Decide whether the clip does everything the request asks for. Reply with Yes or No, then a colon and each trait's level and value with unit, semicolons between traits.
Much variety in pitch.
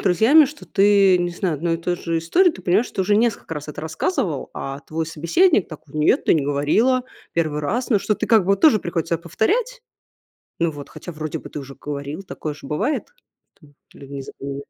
Yes: wide, 6.2 semitones